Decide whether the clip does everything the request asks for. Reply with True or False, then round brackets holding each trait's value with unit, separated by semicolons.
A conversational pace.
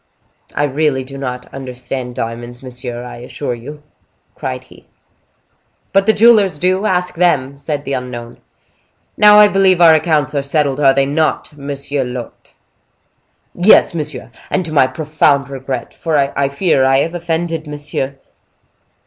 True (150 wpm)